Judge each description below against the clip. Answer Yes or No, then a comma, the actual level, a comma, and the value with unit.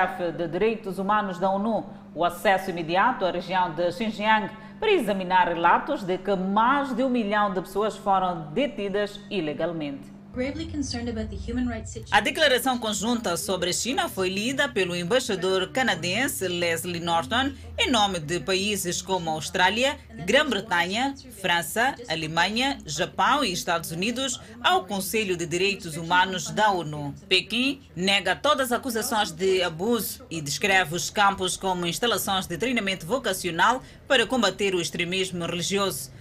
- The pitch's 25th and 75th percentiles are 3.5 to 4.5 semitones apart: Yes, average, 4.1 semitones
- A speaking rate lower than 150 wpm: Yes, average, 135 wpm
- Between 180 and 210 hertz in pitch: Yes, high, 190 Hz